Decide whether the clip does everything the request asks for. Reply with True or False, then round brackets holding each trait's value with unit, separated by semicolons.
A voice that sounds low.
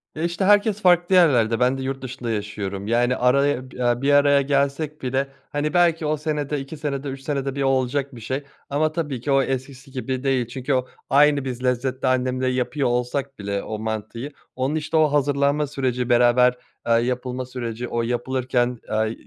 True (130 Hz)